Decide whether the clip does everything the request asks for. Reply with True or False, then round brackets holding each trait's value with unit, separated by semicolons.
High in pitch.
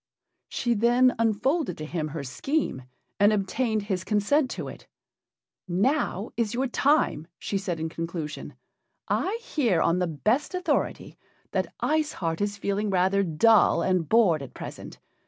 True (205 Hz)